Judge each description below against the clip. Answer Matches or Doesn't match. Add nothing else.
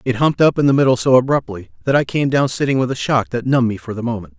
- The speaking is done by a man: Matches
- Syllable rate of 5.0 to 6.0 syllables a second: Doesn't match